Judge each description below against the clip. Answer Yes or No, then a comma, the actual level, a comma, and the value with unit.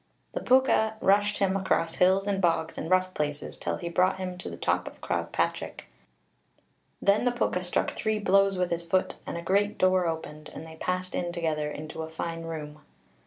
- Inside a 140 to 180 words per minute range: No, average, 200 wpm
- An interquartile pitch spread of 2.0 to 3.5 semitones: Yes, average, 3.0 semitones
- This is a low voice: No, medium, 180 Hz